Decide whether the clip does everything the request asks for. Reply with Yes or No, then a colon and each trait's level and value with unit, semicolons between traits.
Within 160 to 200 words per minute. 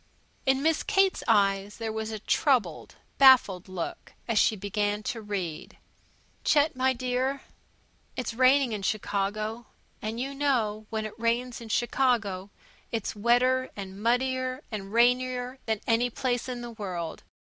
No: average, 140 wpm